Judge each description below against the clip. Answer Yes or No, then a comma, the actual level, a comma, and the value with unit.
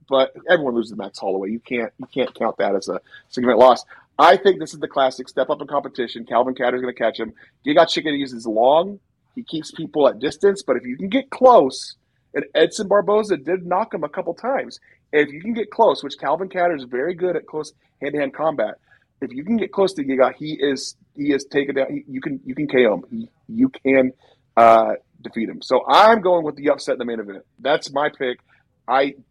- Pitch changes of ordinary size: No, wide, 6.7 semitones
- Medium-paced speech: No, fast, 225 wpm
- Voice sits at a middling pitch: Yes, medium, 145 Hz